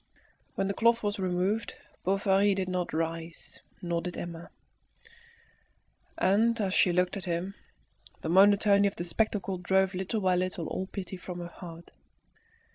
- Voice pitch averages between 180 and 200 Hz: Yes, medium, 185 Hz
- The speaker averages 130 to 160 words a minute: Yes, average, 150 wpm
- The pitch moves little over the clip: Yes, narrow, 2.2 semitones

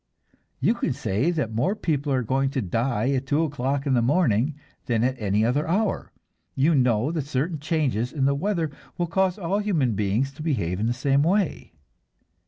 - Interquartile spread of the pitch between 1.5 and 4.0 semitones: No, average, 4.9 semitones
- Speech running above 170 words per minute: Yes, average, 190 wpm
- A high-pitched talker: No, medium, 140 Hz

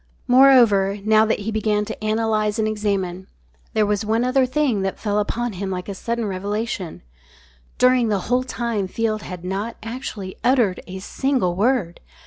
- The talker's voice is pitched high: Yes, high, 215 Hz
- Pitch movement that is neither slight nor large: Yes, average, 3.2 semitones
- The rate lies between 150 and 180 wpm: Yes, average, 165 wpm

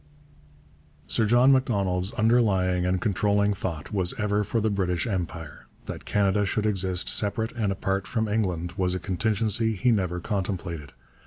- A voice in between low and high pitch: No, low, 100 Hz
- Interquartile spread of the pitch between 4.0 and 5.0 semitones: No, average, 3.0 semitones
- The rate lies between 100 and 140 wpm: No, average, 150 wpm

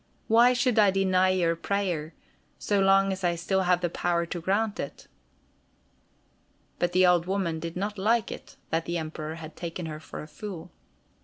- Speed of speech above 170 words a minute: Yes, average, 180 wpm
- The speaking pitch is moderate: Yes, medium, 180 Hz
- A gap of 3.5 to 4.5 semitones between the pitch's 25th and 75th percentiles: No, average, 2.8 semitones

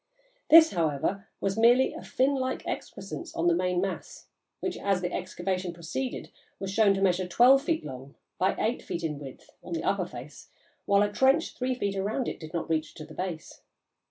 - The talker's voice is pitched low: No, high, 190 Hz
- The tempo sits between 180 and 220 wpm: Yes, average, 195 wpm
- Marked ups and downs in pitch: Yes, wide, 6.2 semitones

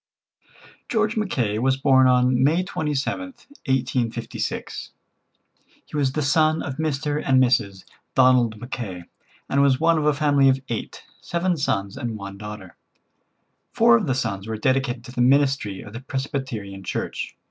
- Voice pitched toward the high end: No, low, 130 Hz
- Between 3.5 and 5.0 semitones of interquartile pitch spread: Yes, average, 4.1 semitones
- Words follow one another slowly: No, average, 150 wpm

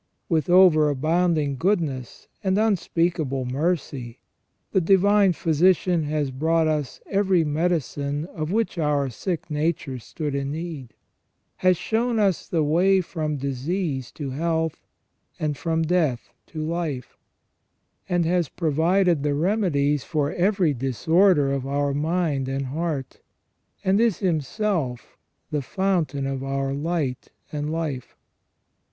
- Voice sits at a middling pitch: Yes, medium, 155 Hz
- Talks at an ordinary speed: No, slow, 125 wpm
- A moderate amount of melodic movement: Yes, average, 4.1 semitones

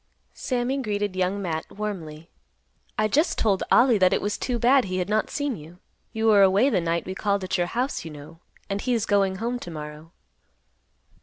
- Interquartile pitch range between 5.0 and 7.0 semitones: No, average, 4.6 semitones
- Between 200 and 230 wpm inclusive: Yes, fast, 205 wpm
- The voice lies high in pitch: Yes, high, 200 Hz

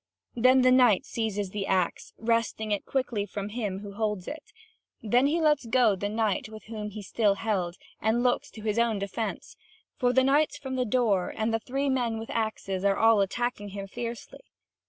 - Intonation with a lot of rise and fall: No, average, 3.3 semitones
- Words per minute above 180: Yes, average, 190 wpm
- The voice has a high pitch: Yes, high, 225 Hz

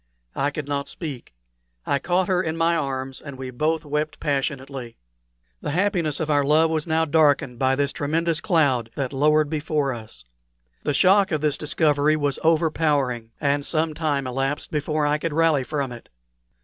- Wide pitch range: No, narrow, 2.5 semitones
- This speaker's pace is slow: No, average, 175 wpm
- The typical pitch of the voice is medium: Yes, medium, 150 Hz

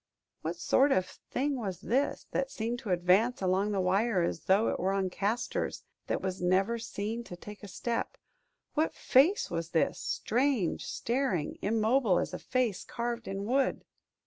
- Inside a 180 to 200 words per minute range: No, average, 170 wpm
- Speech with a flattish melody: No, average, 4.7 semitones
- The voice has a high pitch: Yes, high, 210 Hz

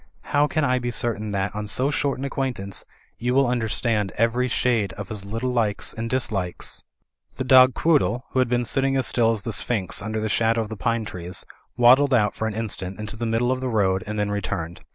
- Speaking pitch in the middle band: No, low, 115 Hz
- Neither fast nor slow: No, fast, 230 wpm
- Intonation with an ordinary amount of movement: Yes, average, 3.5 semitones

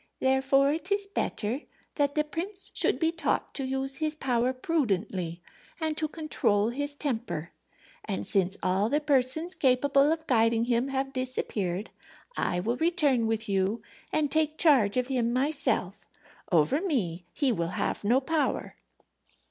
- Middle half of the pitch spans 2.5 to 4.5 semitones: No, wide, 5.4 semitones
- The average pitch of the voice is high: Yes, very high, 265 Hz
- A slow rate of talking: No, average, 150 wpm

